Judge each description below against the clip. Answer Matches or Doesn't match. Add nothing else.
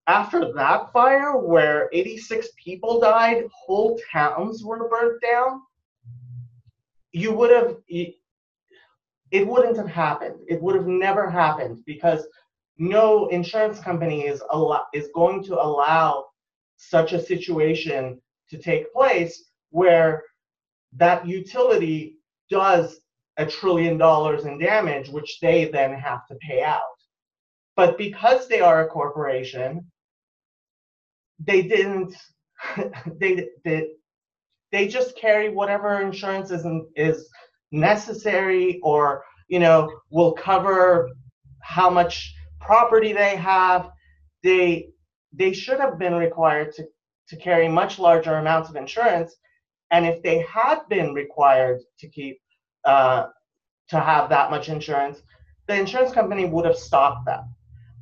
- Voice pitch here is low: Doesn't match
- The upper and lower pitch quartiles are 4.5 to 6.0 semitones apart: Matches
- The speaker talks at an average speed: Doesn't match